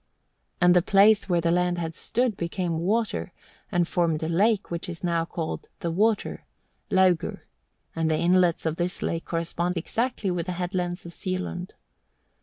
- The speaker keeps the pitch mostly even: Yes, narrow, 2.0 semitones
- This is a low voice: No, medium, 175 Hz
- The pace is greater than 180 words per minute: No, average, 165 wpm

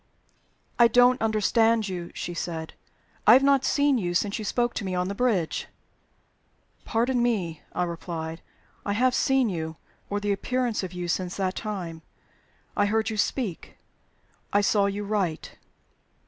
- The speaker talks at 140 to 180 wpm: Yes, average, 160 wpm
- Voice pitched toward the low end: No, high, 205 Hz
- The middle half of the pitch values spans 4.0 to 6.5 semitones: Yes, average, 4.8 semitones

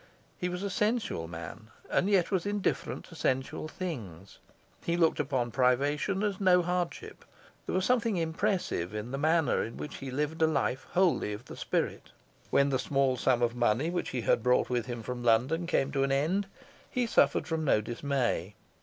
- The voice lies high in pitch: No, medium, 140 Hz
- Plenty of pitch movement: Yes, wide, 6.5 semitones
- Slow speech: No, average, 185 wpm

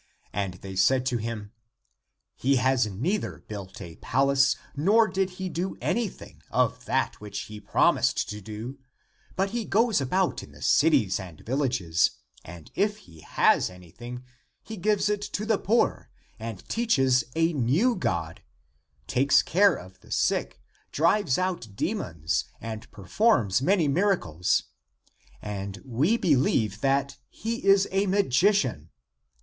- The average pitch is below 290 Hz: Yes, low, 135 Hz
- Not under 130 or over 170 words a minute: Yes, average, 145 wpm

